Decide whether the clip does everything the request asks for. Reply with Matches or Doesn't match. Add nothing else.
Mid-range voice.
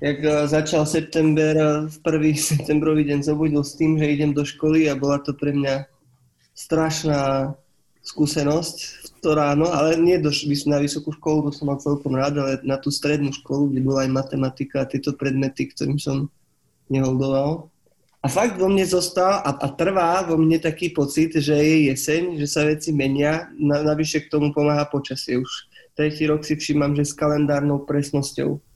Matches